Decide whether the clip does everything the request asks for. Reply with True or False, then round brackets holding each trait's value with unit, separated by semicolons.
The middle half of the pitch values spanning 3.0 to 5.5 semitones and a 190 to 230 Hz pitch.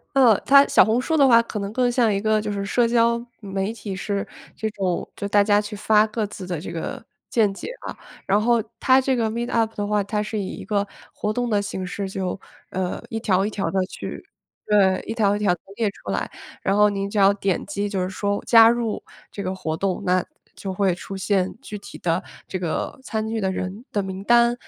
False (2.6 semitones; 205 Hz)